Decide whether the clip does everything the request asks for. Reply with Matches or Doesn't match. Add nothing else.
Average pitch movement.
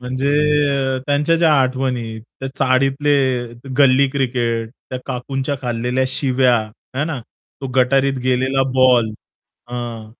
Doesn't match